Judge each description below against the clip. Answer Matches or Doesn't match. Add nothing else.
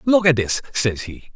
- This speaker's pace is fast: Matches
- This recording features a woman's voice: Doesn't match